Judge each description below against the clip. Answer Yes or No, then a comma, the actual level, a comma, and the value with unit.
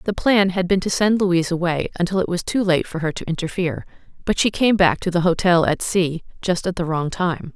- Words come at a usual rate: No, fast, 245 wpm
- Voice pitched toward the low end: No, medium, 180 Hz